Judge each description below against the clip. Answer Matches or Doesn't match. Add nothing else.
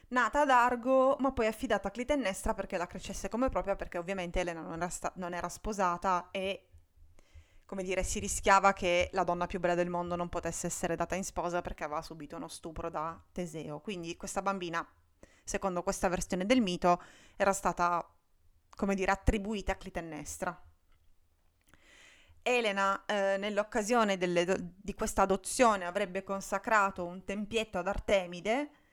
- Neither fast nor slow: Matches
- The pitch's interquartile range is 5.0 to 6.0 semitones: Doesn't match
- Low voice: Doesn't match